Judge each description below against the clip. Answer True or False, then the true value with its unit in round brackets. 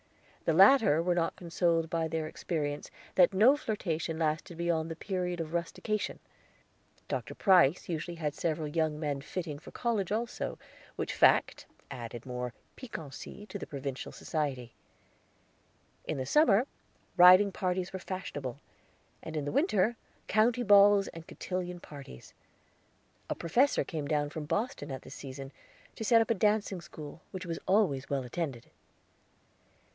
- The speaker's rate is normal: True (145 wpm)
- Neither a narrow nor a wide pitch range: True (4.9 semitones)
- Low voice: False (170 Hz)